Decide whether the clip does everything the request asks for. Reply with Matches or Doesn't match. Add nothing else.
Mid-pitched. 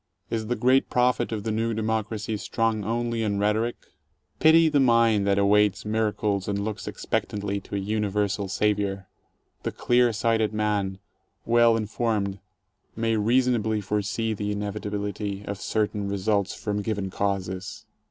Doesn't match